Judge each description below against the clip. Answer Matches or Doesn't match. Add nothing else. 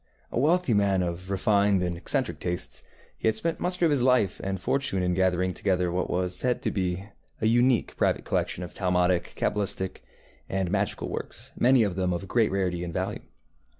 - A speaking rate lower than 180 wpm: Doesn't match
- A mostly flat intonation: Doesn't match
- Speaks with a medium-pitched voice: Doesn't match